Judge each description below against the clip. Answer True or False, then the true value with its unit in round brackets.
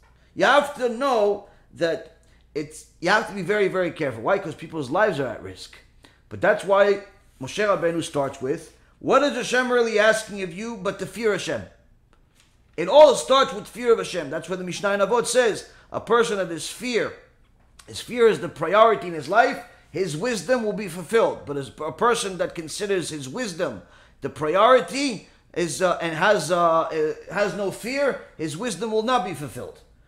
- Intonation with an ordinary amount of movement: False (5.9 semitones)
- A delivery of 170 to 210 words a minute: True (190 wpm)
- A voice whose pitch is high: True (200 Hz)